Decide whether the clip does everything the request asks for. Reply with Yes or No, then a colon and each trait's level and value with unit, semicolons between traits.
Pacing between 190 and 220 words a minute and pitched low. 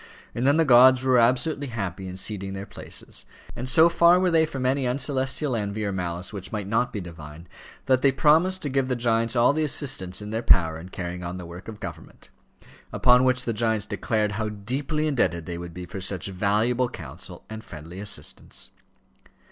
Yes: average, 200 wpm; low, 115 Hz